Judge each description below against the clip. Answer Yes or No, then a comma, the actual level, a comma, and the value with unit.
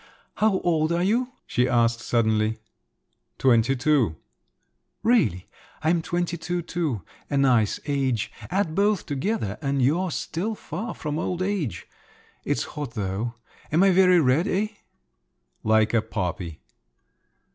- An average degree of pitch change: No, wide, 7.6 semitones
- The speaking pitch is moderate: Yes, medium, 150 Hz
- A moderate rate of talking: No, slow, 130 wpm